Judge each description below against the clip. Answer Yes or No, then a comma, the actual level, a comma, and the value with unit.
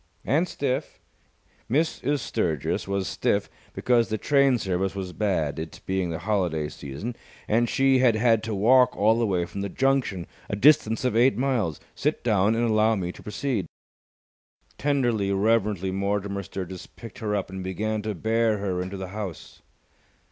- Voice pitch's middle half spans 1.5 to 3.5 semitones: No, average, 4.0 semitones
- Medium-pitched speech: No, low, 105 Hz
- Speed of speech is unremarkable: Yes, average, 165 wpm